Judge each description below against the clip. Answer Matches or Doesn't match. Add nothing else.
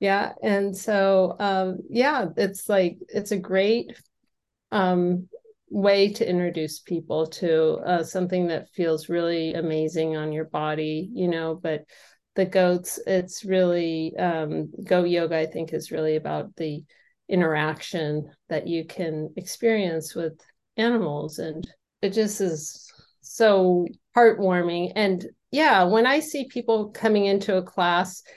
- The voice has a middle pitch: Matches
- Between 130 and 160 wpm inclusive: Matches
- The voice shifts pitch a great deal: Doesn't match